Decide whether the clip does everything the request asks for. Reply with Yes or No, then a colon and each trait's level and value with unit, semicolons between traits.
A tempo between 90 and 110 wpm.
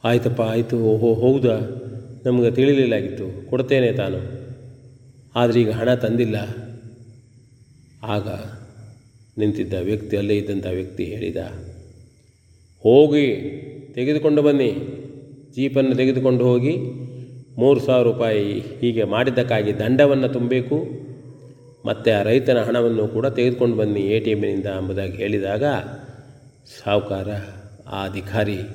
Yes: average, 100 wpm